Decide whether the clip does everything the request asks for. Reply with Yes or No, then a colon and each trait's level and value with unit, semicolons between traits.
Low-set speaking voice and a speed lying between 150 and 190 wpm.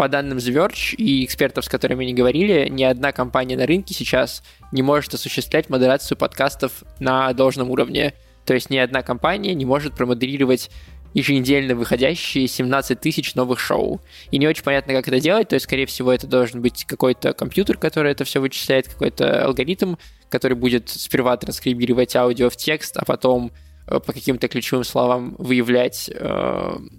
Yes: low, 130 Hz; fast, 160 wpm